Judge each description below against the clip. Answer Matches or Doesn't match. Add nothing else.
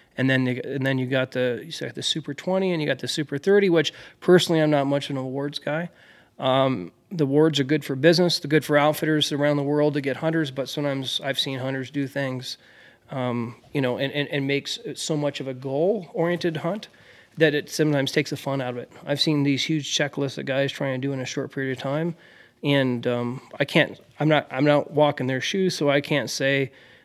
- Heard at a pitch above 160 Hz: Doesn't match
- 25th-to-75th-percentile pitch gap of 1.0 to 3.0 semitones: Matches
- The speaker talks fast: Matches